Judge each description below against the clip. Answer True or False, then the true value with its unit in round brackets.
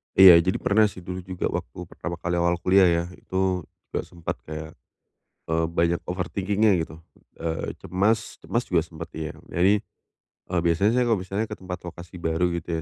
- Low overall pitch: True (90 Hz)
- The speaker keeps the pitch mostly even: True (2.2 semitones)